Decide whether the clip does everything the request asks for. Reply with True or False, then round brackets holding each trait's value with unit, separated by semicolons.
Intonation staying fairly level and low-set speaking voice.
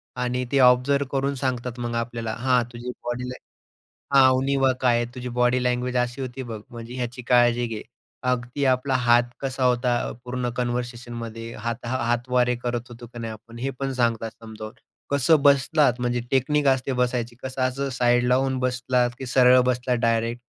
True (1.3 semitones; 125 Hz)